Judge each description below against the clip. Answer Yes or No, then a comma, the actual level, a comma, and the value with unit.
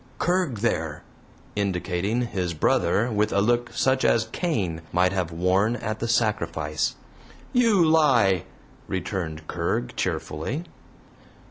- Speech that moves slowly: Yes, slow, 115 wpm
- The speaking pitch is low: Yes, low, 100 Hz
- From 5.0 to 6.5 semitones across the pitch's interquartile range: Yes, wide, 5.6 semitones